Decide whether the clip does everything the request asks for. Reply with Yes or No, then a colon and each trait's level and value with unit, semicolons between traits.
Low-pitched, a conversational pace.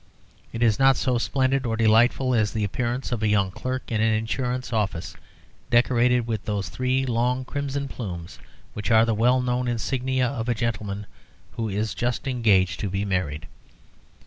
Yes: low, 115 Hz; average, 170 wpm